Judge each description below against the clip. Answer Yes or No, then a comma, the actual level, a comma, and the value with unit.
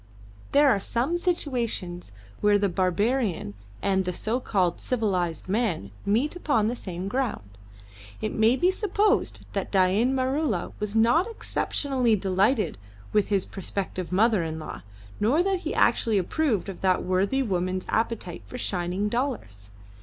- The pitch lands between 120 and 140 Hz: No, high, 210 Hz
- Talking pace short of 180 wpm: Yes, average, 145 wpm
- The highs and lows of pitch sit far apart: Yes, wide, 5.8 semitones